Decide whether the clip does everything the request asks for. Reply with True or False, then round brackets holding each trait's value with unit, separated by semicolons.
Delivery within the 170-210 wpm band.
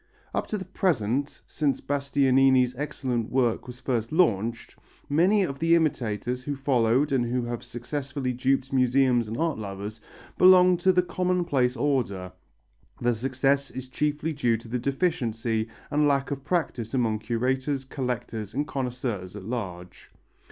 False (145 wpm)